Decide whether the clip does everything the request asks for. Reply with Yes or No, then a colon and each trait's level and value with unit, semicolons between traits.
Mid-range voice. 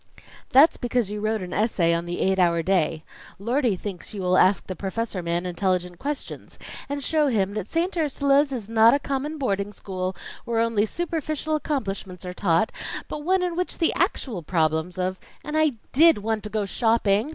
No: high, 215 Hz